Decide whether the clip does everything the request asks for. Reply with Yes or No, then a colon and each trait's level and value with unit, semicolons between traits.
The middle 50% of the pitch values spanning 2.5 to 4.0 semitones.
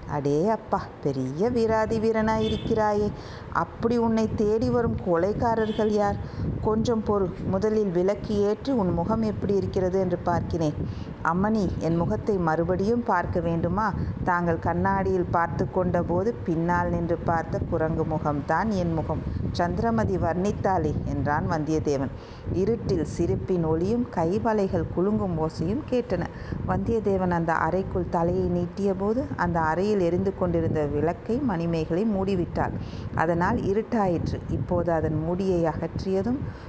No: average, 4.5 semitones